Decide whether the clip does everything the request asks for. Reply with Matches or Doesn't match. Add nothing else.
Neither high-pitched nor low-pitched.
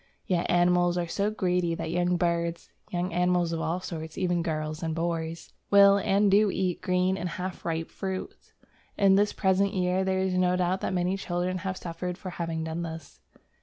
Matches